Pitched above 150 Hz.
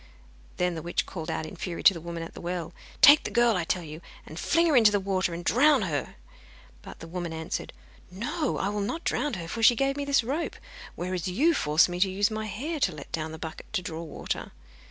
Yes: medium, 185 Hz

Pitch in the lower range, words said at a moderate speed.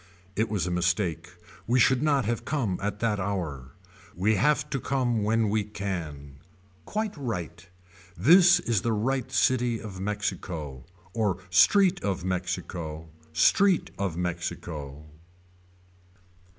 No: low, 100 Hz; slow, 125 wpm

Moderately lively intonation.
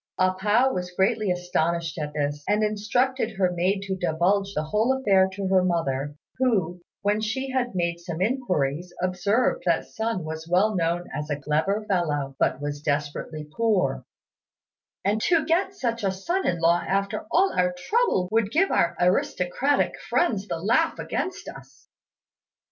Yes: average, 4.6 semitones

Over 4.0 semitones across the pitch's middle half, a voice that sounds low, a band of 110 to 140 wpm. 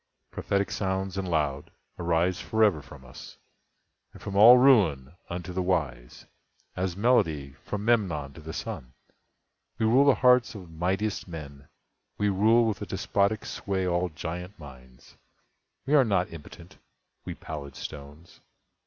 Yes: wide, 5.4 semitones; very low, 90 Hz; slow, 135 wpm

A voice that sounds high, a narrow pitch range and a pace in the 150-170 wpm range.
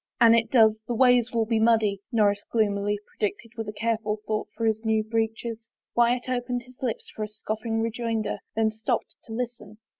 No: high, 225 Hz; narrow, 1.5 semitones; average, 200 wpm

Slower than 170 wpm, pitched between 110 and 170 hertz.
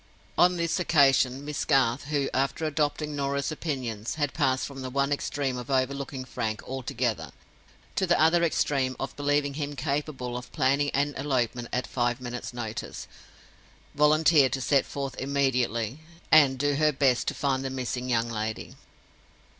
Yes: average, 155 wpm; low, 135 Hz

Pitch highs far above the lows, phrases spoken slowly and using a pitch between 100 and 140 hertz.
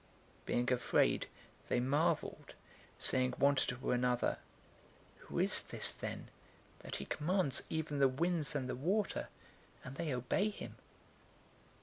No: average, 4.0 semitones; slow, 125 wpm; low, 135 Hz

